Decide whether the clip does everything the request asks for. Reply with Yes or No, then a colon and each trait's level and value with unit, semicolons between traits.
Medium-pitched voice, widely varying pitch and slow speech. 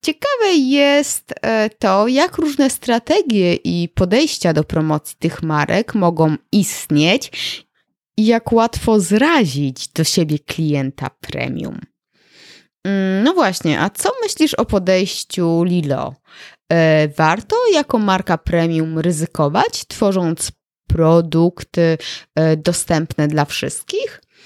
Yes: medium, 175 Hz; wide, 6.3 semitones; slow, 100 wpm